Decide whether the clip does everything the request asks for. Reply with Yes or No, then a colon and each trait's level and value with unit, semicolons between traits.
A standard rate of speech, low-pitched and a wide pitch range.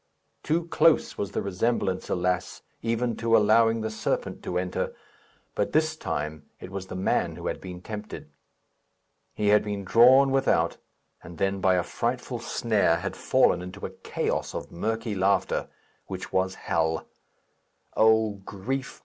No: average, 150 wpm; low, 105 Hz; average, 3.7 semitones